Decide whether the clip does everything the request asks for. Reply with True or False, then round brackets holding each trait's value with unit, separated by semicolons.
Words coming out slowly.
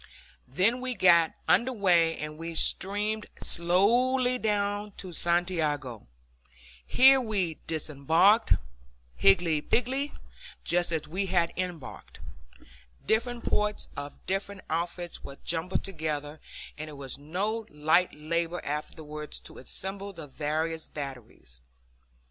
True (115 wpm)